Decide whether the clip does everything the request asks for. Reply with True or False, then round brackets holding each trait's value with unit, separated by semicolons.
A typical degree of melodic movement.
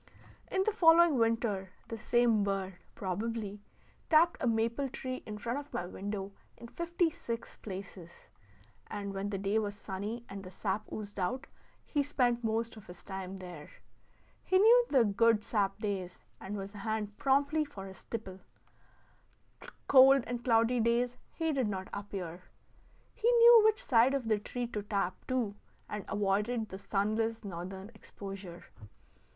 True (4.0 semitones)